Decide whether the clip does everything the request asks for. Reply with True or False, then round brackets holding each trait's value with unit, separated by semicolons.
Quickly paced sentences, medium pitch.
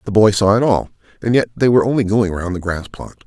False (275 wpm; 105 Hz)